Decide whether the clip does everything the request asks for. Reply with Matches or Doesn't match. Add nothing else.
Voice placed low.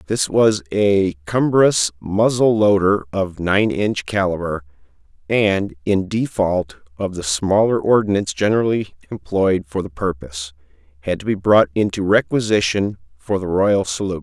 Matches